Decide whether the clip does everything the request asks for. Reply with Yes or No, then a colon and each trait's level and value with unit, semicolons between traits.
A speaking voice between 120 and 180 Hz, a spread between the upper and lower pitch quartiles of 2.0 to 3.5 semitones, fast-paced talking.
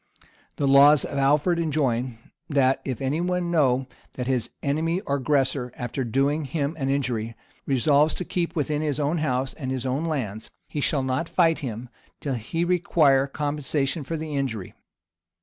No: medium, 140 Hz; average, 2.9 semitones; average, 165 wpm